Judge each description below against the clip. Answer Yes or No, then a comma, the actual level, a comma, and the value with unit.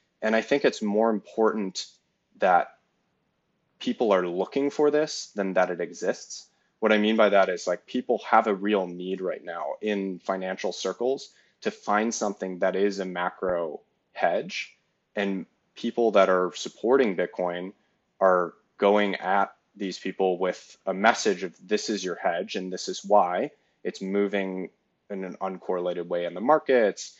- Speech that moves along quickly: No, average, 160 wpm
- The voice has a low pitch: Yes, low, 100 Hz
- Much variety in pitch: No, narrow, 2.6 semitones